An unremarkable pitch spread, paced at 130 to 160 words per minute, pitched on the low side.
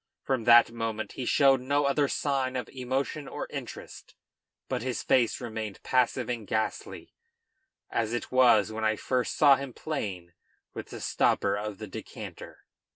Yes: average, 3.4 semitones; average, 155 wpm; low, 120 Hz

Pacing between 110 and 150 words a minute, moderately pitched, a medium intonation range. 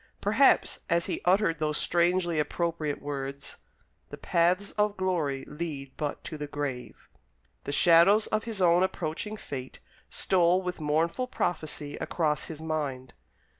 Yes: slow, 135 wpm; medium, 165 Hz; average, 3.7 semitones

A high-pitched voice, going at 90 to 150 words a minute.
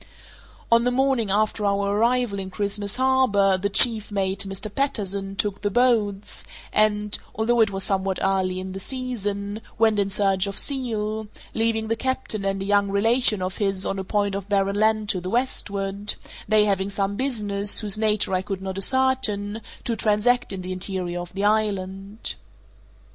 No: high, 205 Hz; average, 175 wpm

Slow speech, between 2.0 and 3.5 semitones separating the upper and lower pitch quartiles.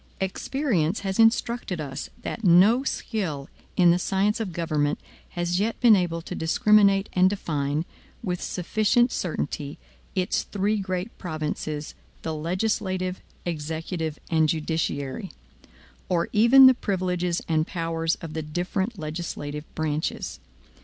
No: slow, 125 wpm; average, 4.1 semitones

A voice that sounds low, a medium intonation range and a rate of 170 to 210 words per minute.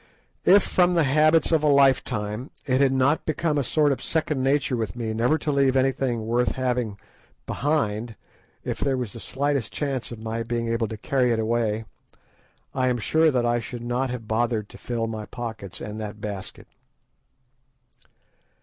Yes: low, 125 Hz; average, 3.6 semitones; average, 175 wpm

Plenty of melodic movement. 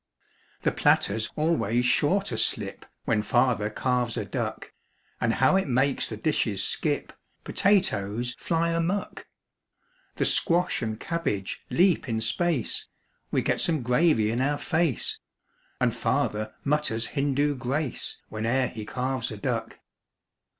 Yes: wide, 5.7 semitones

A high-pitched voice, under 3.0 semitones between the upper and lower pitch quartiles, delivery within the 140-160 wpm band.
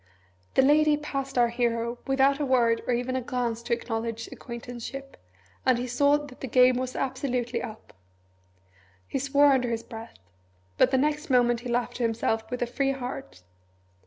No: very high, 250 Hz; narrow, 2.5 semitones; average, 175 wpm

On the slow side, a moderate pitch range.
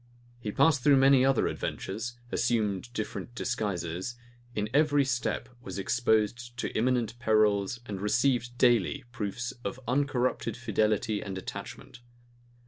Yes: slow, 125 wpm; average, 3.1 semitones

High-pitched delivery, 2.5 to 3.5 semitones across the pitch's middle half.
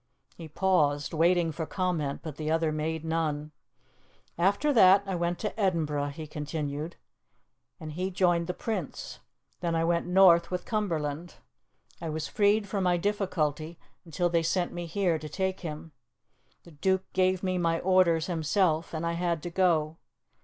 No: medium, 170 Hz; average, 2.9 semitones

